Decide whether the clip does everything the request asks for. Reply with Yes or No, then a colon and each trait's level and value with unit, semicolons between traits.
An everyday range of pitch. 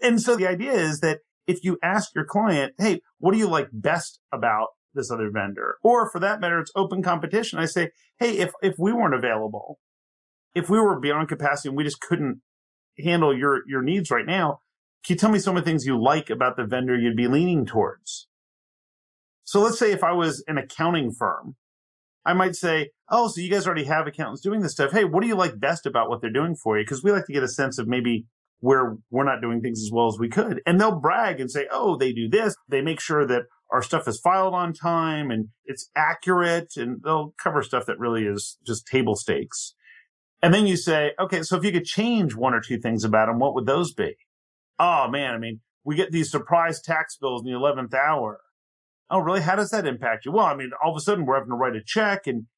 No: wide, 6.6 semitones